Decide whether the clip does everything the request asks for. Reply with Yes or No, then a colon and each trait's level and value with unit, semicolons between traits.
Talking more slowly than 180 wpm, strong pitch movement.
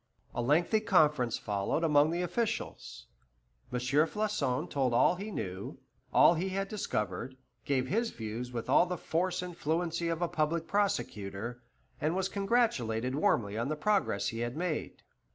Yes: average, 155 wpm; wide, 6.8 semitones